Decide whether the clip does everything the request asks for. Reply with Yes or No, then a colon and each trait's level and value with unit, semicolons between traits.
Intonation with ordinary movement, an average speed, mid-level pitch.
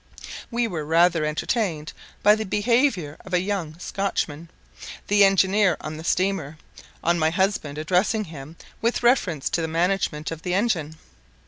Yes: average, 4.4 semitones; average, 150 wpm; medium, 180 Hz